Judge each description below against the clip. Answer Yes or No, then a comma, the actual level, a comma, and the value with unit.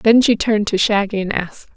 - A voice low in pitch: No, high, 210 Hz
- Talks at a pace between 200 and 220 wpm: No, fast, 240 wpm